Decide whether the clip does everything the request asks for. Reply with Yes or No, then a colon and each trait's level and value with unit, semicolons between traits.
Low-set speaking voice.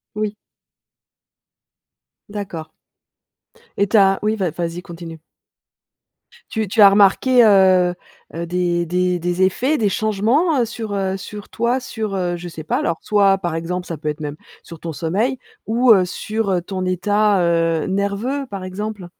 No: high, 195 Hz